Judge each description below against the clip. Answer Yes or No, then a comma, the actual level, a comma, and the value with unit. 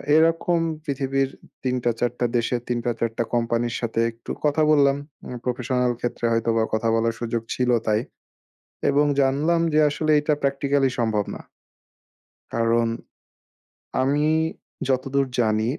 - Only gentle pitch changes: No, average, 3.3 semitones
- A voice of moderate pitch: No, low, 125 Hz